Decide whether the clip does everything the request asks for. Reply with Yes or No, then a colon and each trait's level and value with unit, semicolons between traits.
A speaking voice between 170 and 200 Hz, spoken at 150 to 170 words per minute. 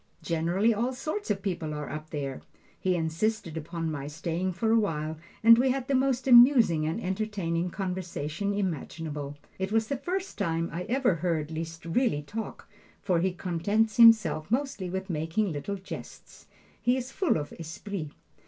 Yes: medium, 185 Hz; average, 165 wpm